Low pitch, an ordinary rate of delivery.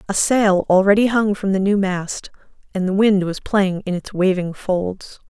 No: high, 195 Hz; average, 190 wpm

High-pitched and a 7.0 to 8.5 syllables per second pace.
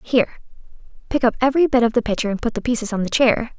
Yes: high, 240 Hz; 7.6 syllables/s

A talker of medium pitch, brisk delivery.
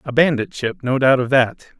No: low, 130 Hz; fast, 235 wpm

